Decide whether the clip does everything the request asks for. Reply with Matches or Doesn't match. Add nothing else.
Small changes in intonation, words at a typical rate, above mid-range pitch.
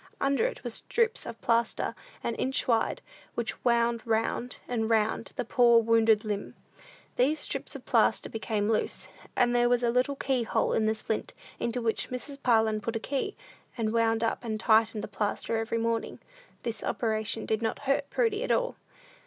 Matches